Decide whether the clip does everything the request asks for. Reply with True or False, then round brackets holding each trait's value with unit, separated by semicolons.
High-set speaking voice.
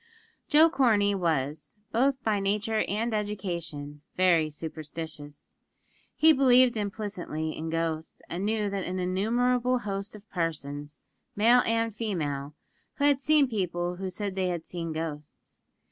True (195 Hz)